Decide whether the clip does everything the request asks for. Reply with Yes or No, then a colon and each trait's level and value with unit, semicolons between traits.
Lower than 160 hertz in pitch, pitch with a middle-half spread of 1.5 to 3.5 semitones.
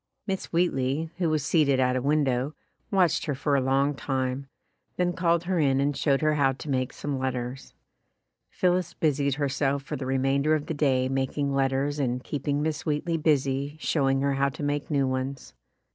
Yes: medium, 140 Hz; narrow, 2.4 semitones